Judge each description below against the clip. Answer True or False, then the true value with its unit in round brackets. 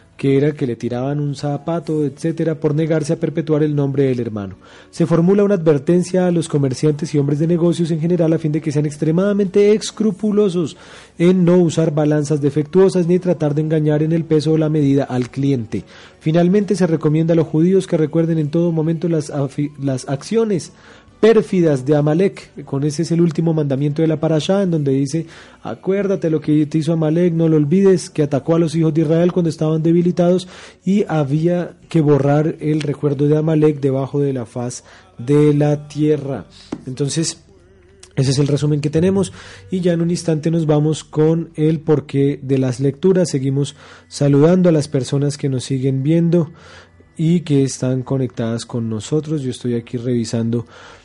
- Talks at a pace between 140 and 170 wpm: False (185 wpm)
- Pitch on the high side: False (155 Hz)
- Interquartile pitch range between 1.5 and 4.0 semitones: True (3.2 semitones)